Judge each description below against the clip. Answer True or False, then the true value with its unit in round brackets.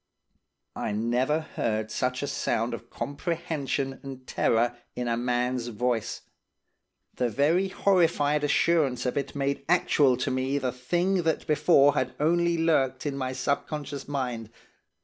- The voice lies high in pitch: False (135 Hz)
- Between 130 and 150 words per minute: True (140 wpm)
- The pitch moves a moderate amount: True (3.5 semitones)